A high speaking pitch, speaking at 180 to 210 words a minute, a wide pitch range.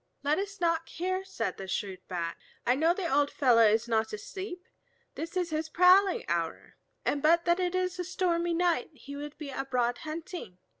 Yes: very high, 320 Hz; average, 190 wpm; wide, 6.3 semitones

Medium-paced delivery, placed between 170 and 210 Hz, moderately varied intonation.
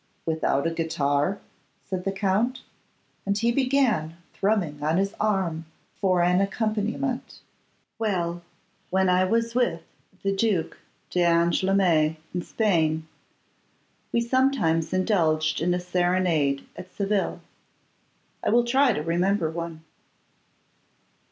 No: slow, 115 wpm; medium, 185 Hz; average, 4.3 semitones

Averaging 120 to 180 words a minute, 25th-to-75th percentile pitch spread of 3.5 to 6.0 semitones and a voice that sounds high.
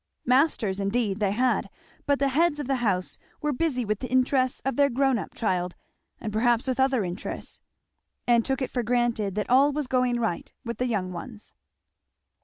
No: average, 190 wpm; average, 3.9 semitones; high, 245 Hz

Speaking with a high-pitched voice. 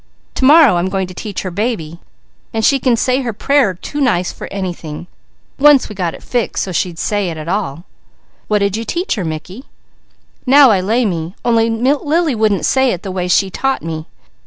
Yes: high, 205 Hz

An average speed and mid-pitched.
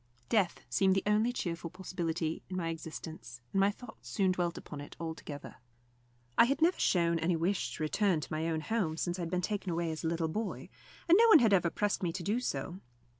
No: fast, 225 wpm; medium, 175 Hz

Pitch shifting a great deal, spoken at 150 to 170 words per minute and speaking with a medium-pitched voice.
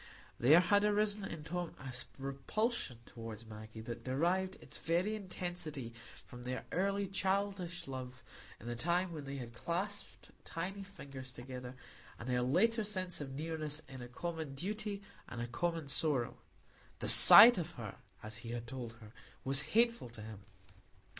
Yes: wide, 7.2 semitones; average, 160 wpm; medium, 150 Hz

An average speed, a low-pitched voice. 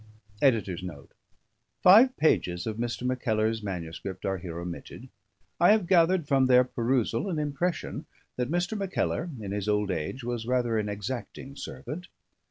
Yes: average, 150 wpm; low, 120 Hz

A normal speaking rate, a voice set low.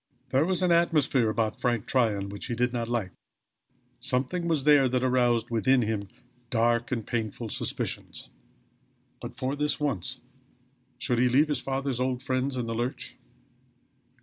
Yes: average, 155 wpm; low, 125 Hz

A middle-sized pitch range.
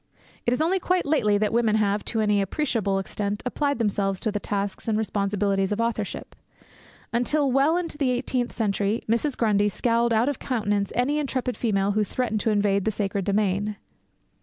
Yes: average, 3.6 semitones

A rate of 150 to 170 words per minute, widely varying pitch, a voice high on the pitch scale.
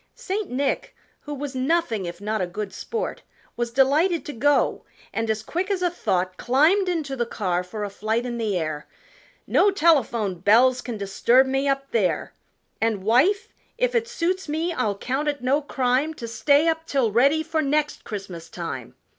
No: average, 180 wpm; wide, 6.6 semitones; very high, 260 Hz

